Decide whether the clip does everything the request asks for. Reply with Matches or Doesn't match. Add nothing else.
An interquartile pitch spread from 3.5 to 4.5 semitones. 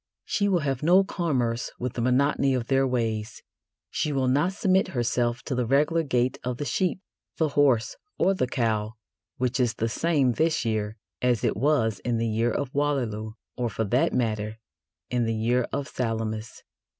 Matches